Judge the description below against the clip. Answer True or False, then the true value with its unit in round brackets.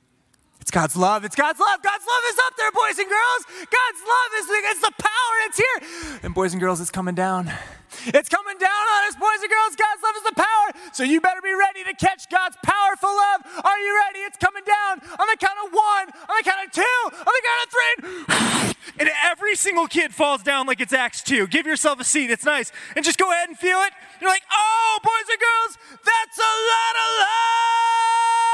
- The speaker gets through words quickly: True (225 wpm)